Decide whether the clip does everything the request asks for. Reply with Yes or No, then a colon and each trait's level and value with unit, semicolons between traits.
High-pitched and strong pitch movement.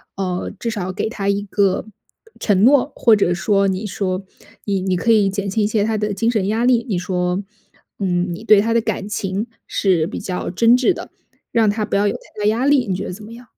No: high, 205 Hz; average, 3.0 semitones